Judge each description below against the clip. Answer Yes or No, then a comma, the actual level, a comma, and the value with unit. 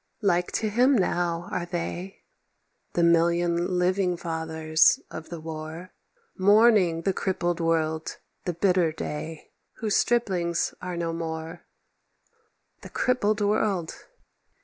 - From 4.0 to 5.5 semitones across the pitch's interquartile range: No, average, 2.7 semitones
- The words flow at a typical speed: No, slow, 115 wpm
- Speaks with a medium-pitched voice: Yes, medium, 175 Hz